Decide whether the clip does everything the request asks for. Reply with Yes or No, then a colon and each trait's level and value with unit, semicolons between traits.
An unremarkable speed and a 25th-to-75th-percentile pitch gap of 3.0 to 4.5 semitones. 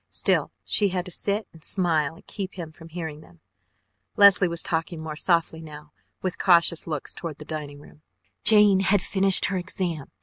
Yes: average, 180 wpm; average, 3.3 semitones